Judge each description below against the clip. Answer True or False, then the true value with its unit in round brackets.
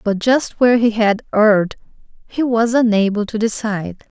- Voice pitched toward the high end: True (220 Hz)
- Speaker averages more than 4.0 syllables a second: True (5.0 syllables/s)